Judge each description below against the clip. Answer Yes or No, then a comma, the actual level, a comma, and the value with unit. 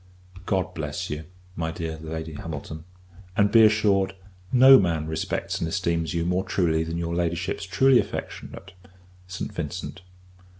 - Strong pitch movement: No, average, 3.3 semitones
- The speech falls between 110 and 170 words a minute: Yes, average, 140 wpm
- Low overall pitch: Yes, very low, 85 Hz